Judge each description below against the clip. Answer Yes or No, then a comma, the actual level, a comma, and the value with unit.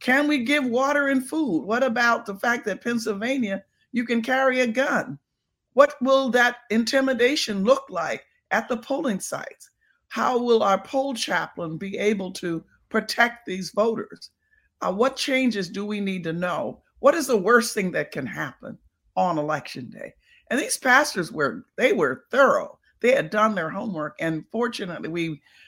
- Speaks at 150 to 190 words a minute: Yes, average, 170 wpm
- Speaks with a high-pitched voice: Yes, high, 235 Hz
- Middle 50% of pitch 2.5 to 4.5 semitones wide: No, average, 5.2 semitones